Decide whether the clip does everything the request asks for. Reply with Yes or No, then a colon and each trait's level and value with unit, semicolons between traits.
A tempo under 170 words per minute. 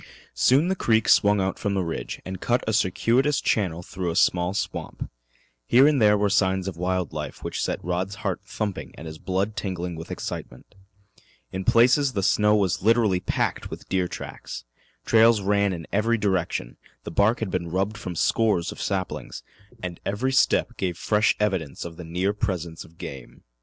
No: average, 180 wpm